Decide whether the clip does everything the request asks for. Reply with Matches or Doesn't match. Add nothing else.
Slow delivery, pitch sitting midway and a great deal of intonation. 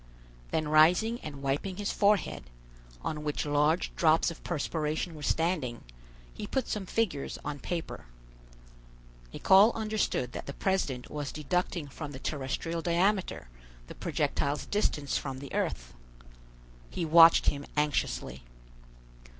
Doesn't match